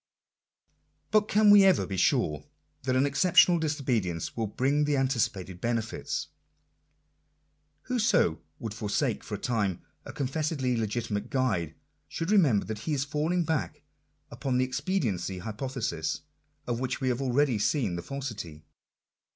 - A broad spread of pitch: Yes, wide, 6.0 semitones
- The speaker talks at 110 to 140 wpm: Yes, slow, 135 wpm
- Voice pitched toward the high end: No, low, 130 Hz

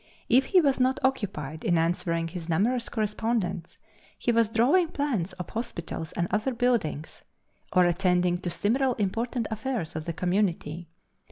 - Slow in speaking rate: No, average, 150 wpm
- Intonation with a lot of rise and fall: Yes, wide, 6.0 semitones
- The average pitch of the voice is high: Yes, high, 205 Hz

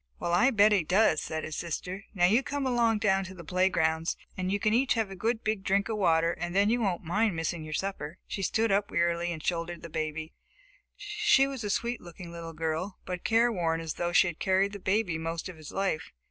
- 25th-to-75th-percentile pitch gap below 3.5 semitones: No, average, 4.3 semitones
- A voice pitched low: No, medium, 185 Hz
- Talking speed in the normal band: No, fast, 230 wpm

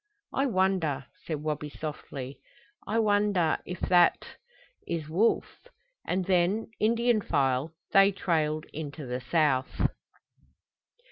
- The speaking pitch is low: No, medium, 165 Hz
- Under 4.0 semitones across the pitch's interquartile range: No, average, 4.7 semitones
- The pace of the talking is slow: Yes, slow, 110 wpm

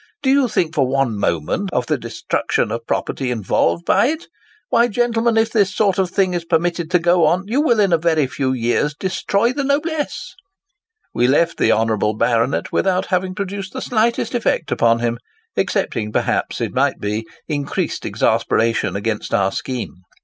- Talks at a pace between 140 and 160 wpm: No, average, 175 wpm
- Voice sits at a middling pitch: Yes, medium, 170 Hz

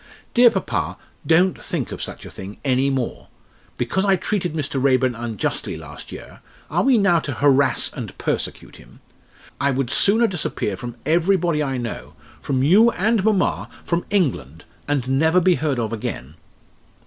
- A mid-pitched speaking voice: Yes, medium, 145 Hz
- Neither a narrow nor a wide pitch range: No, wide, 6.4 semitones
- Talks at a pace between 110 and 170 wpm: Yes, average, 160 wpm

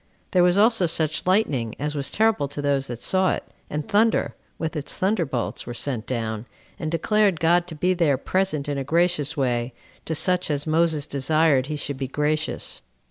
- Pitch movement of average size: Yes, average, 4.3 semitones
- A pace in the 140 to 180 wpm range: No, average, 190 wpm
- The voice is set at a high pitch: No, medium, 155 Hz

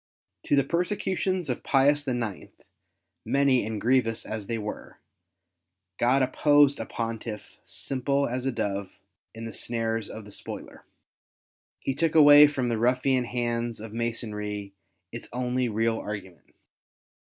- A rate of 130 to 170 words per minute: Yes, slow, 135 wpm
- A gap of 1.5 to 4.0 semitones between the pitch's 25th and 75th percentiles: Yes, average, 3.6 semitones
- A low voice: Yes, low, 120 Hz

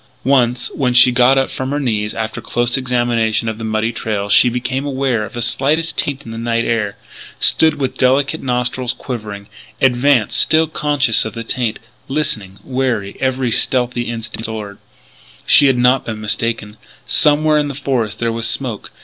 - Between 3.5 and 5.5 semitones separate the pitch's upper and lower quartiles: No, average, 3.1 semitones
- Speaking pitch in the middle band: No, low, 125 Hz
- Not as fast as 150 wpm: No, average, 175 wpm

